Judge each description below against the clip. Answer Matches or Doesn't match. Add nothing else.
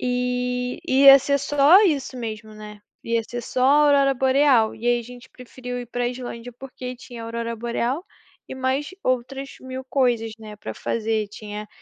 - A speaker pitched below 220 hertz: Doesn't match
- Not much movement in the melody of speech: Matches